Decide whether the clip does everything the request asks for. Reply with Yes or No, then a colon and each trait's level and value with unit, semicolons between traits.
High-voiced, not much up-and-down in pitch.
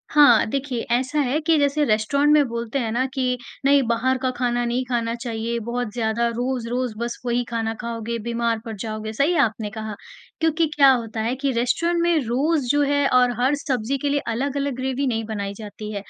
No: high, 245 Hz; average, 3.3 semitones